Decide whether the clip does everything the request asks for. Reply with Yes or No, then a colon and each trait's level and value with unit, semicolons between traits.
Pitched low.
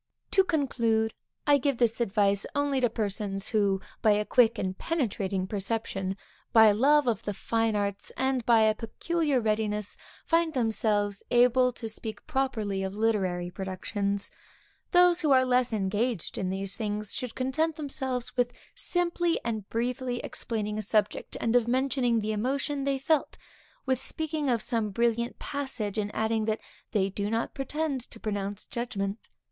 No: high, 225 Hz